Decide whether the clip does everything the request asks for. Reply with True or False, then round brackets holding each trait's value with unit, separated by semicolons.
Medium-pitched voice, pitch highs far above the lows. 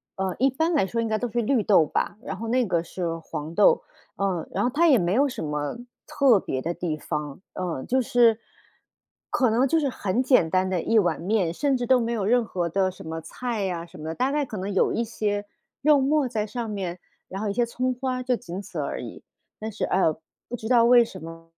False (215 Hz; 5.7 semitones)